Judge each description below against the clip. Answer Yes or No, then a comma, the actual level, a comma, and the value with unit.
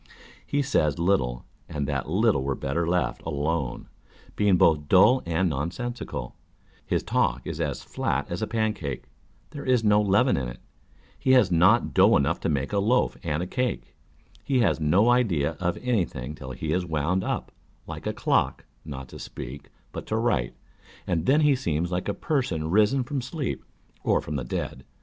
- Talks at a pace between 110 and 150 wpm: No, average, 180 wpm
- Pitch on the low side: Yes, very low, 90 Hz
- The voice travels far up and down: Yes, wide, 7.7 semitones